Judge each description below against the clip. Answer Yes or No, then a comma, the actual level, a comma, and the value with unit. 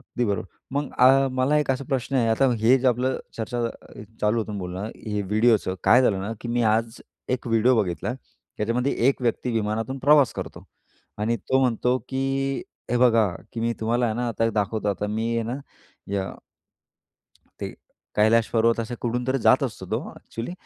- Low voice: Yes, low, 115 Hz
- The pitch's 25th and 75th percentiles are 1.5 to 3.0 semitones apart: Yes, narrow, 2.6 semitones